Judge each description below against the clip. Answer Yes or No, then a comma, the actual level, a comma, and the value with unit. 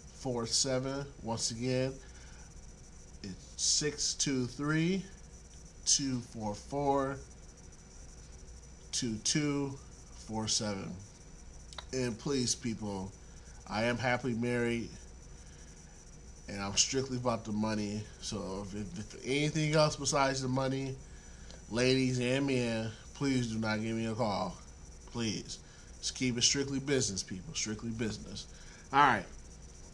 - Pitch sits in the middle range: No, low, 115 Hz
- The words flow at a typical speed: No, slow, 125 wpm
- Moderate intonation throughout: No, wide, 5.7 semitones